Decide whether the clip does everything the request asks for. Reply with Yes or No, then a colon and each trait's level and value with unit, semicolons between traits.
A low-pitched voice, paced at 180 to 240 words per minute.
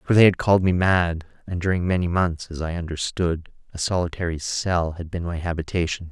Yes: very low, 85 Hz; average, 195 wpm